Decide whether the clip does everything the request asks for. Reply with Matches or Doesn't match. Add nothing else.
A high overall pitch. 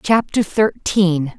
Matches